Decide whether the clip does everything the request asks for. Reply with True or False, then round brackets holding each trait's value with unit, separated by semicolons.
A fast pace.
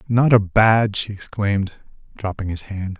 False (160 wpm)